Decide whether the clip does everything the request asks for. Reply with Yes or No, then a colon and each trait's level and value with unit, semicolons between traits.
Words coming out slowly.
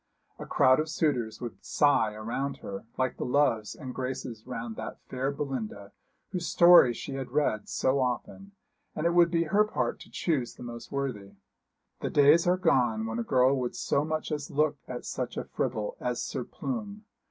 No: average, 185 wpm